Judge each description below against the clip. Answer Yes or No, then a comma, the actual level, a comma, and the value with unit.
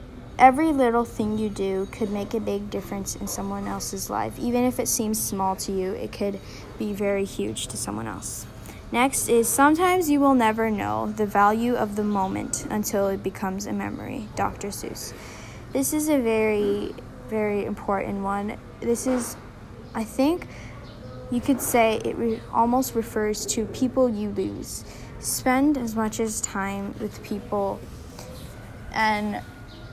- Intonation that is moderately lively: Yes, average, 3.8 semitones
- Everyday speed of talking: Yes, average, 155 wpm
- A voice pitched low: No, high, 210 Hz